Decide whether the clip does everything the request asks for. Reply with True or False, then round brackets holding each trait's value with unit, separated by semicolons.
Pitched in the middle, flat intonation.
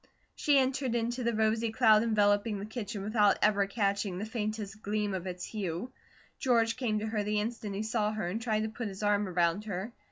False (215 Hz; 2.1 semitones)